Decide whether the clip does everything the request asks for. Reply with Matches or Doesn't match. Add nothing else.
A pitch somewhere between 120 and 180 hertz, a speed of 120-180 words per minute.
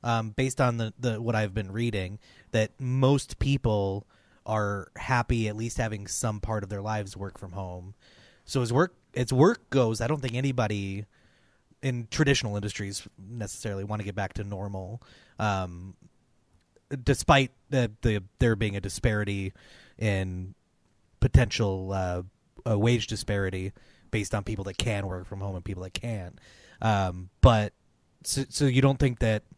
Doesn't match